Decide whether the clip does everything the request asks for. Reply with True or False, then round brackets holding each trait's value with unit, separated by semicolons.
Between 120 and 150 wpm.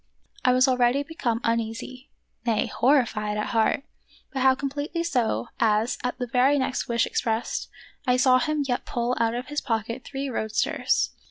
False (165 wpm)